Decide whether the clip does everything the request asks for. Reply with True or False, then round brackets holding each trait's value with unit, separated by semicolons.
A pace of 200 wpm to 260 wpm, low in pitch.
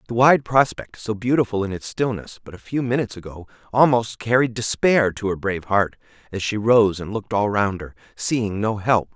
True (205 wpm; 110 Hz)